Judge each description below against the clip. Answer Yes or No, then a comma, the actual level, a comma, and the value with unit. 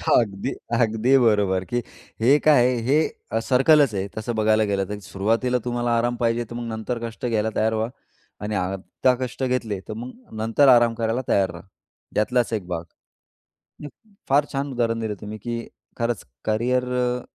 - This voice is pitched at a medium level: No, low, 115 Hz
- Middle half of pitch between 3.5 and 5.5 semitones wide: No, narrow, 2.5 semitones